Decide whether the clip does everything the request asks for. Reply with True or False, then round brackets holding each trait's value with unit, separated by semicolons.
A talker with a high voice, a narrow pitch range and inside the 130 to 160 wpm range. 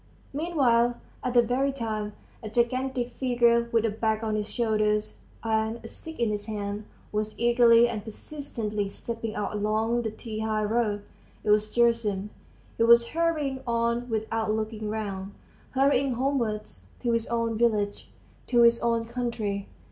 True (230 Hz; 1.9 semitones; 155 wpm)